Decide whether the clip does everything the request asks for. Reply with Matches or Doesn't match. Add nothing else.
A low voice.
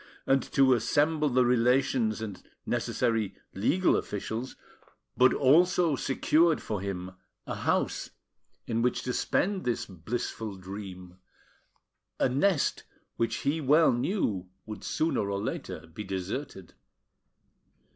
Matches